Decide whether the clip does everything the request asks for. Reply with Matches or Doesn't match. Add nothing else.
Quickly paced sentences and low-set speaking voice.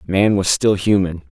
Doesn't match